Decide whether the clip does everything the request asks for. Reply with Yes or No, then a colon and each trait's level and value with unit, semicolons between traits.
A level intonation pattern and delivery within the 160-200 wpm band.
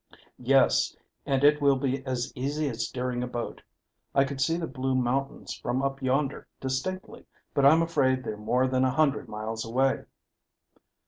Yes: narrow, 1.8 semitones; average, 170 wpm